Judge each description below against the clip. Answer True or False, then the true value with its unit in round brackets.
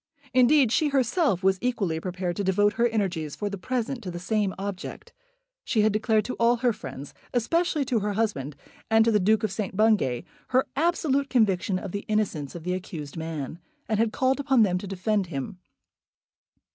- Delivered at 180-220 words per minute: True (190 wpm)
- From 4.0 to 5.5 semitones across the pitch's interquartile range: True (4.6 semitones)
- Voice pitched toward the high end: True (210 Hz)